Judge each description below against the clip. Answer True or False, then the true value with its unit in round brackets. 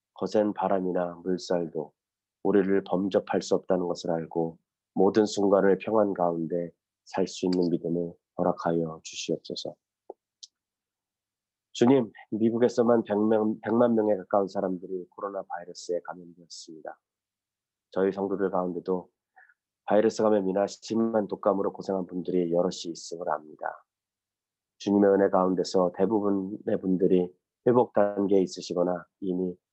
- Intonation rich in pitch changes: False (2.5 semitones)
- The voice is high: False (95 Hz)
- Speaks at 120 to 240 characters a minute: False (295 characters per minute)